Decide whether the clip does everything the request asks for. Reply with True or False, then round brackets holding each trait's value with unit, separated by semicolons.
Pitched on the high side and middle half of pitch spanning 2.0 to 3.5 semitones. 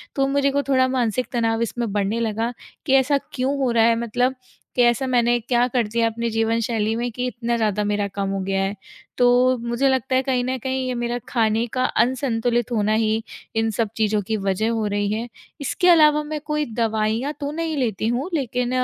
True (235 Hz; 2.8 semitones)